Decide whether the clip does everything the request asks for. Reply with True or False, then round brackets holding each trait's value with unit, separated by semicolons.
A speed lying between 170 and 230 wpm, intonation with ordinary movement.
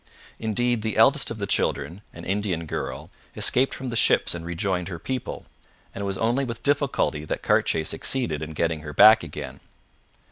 False (180 wpm; 6.3 semitones)